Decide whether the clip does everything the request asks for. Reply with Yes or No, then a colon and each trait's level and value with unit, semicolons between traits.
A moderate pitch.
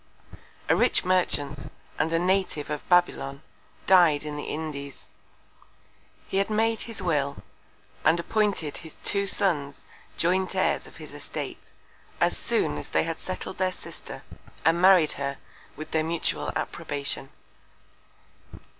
Yes: medium, 165 Hz